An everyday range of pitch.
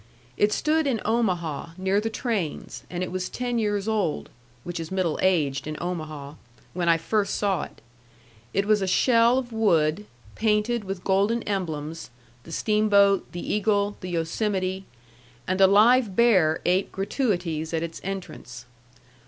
Yes: average, 4.1 semitones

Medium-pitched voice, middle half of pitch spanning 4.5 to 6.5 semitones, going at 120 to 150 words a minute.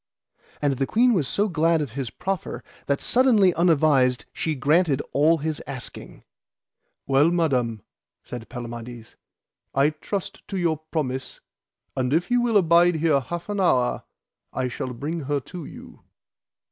Yes: medium, 155 Hz; average, 5.0 semitones; average, 145 wpm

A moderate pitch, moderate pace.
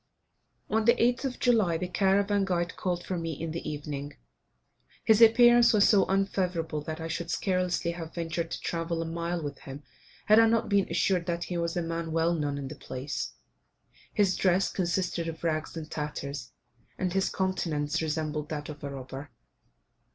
Yes: medium, 170 Hz; average, 180 wpm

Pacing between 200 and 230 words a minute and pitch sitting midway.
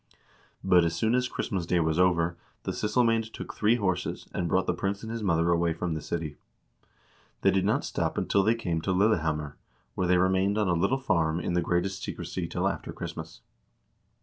No: fast, 205 wpm; very low, 90 Hz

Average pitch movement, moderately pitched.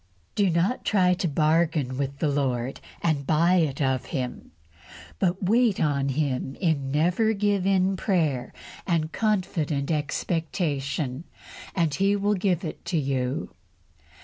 Yes: average, 4.9 semitones; medium, 160 Hz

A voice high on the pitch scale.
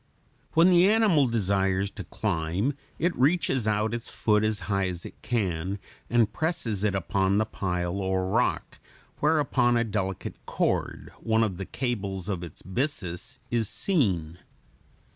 No: low, 105 Hz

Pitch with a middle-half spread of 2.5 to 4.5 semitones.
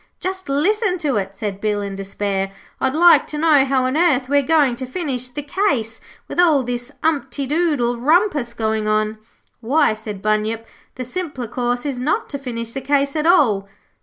No: wide, 5.4 semitones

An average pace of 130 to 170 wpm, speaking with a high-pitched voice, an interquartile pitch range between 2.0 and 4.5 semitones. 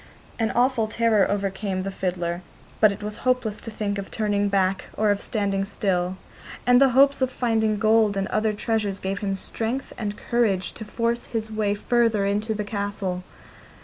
No: average, 180 wpm; high, 210 Hz; narrow, 2.4 semitones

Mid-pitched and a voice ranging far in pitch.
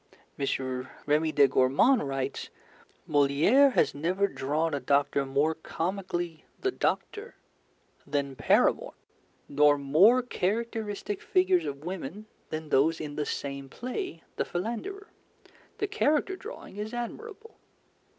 Yes: medium, 165 Hz; wide, 8.4 semitones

